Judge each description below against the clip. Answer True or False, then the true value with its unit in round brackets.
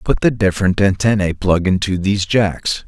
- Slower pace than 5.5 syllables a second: True (5.1 syllables/s)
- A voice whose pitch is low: True (95 Hz)